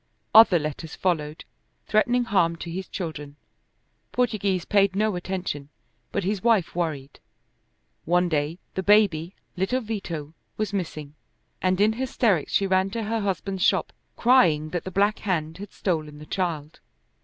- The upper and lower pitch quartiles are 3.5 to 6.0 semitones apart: Yes, average, 4.4 semitones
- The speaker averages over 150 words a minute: No, average, 145 wpm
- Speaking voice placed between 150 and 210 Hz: Yes, medium, 185 Hz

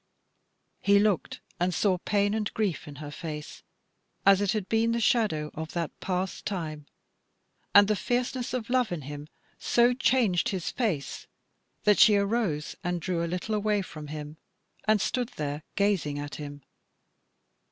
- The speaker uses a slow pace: No, average, 160 wpm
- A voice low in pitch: No, high, 190 Hz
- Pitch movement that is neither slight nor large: No, wide, 5.8 semitones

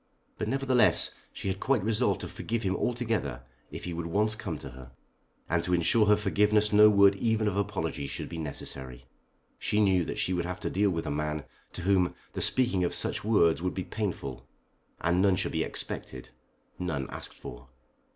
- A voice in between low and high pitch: No, very low, 95 Hz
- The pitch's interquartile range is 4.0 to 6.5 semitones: Yes, average, 4.4 semitones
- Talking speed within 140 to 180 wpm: No, average, 195 wpm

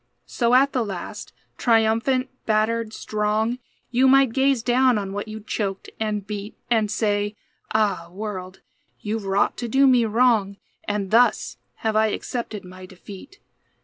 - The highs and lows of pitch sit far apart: No, average, 2.8 semitones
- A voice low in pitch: No, high, 220 Hz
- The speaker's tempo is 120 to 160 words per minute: Yes, average, 145 wpm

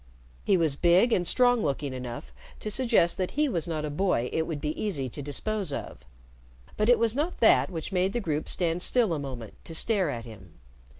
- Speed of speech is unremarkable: No, fast, 215 wpm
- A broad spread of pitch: Yes, wide, 6.8 semitones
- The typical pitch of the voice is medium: Yes, medium, 170 Hz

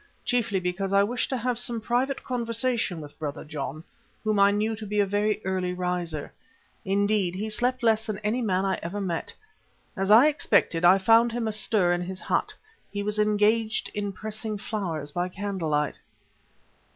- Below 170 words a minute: No, average, 175 wpm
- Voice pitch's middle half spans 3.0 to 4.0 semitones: Yes, average, 3.5 semitones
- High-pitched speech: Yes, high, 205 Hz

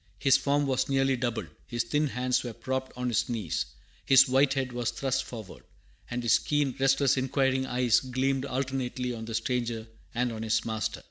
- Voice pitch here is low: Yes, low, 130 Hz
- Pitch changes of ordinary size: No, narrow, 2.2 semitones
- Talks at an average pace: Yes, average, 185 wpm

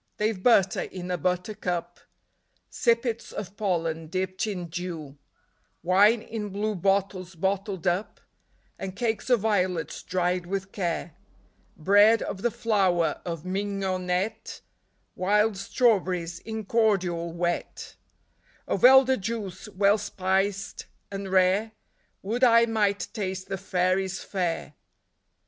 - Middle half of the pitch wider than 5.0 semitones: No, average, 2.8 semitones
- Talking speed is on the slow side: Yes, slow, 120 wpm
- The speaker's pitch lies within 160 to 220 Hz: Yes, high, 190 Hz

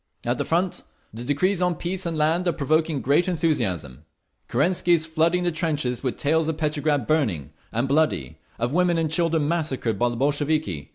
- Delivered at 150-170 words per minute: No, average, 180 wpm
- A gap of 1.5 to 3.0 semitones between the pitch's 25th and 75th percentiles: No, average, 4.2 semitones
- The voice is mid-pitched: Yes, medium, 155 Hz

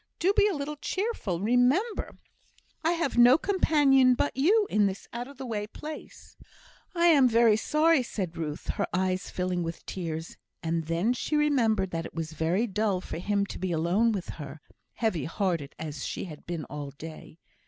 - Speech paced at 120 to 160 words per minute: No, average, 185 wpm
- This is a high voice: Yes, high, 210 Hz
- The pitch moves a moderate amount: No, wide, 8.7 semitones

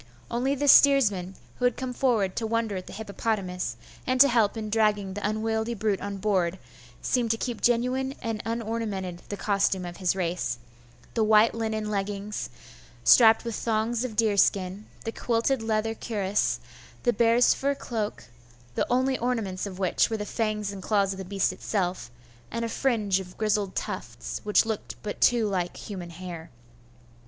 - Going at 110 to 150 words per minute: No, average, 170 wpm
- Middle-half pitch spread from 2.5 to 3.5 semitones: Yes, average, 2.9 semitones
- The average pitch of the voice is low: No, high, 215 Hz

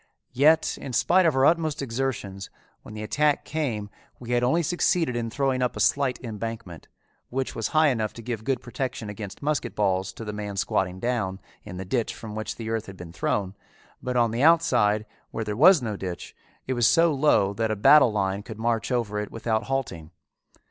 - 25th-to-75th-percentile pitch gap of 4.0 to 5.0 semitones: Yes, average, 4.3 semitones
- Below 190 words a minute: No, fast, 205 wpm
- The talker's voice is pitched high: No, low, 115 Hz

